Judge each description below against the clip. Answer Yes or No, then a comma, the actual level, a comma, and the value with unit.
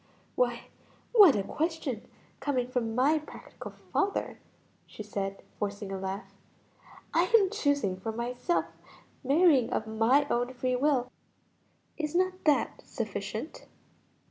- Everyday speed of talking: No, slow, 120 wpm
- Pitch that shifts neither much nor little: No, wide, 5.8 semitones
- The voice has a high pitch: Yes, very high, 255 Hz